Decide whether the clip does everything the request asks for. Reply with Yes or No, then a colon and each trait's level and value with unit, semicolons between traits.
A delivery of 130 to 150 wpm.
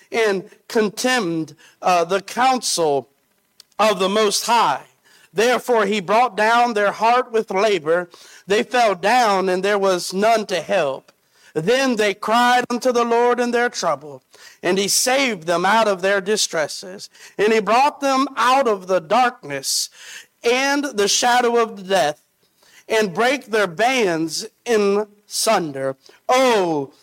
Yes: average, 140 wpm